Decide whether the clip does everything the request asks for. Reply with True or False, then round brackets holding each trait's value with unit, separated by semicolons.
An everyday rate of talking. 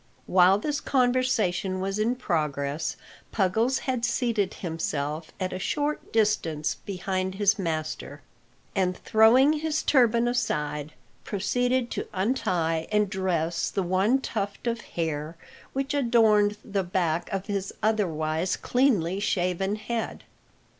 False (120 wpm)